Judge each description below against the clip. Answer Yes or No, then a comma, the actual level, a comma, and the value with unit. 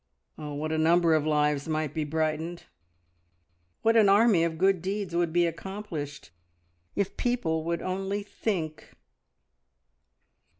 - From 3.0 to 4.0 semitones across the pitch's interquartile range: Yes, average, 3.7 semitones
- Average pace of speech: No, slow, 130 wpm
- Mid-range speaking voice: Yes, medium, 170 Hz